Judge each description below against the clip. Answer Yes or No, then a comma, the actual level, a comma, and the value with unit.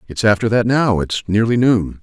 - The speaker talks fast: No, average, 180 wpm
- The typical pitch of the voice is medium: No, low, 110 Hz